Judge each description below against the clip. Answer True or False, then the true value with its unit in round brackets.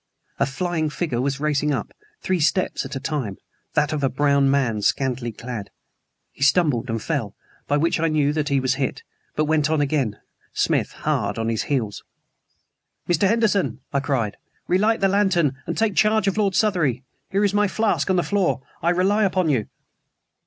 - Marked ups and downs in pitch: True (5.8 semitones)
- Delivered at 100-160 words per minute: False (185 wpm)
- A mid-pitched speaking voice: True (150 Hz)